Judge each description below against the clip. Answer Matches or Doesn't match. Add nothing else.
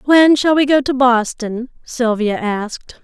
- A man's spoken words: Doesn't match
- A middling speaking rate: Matches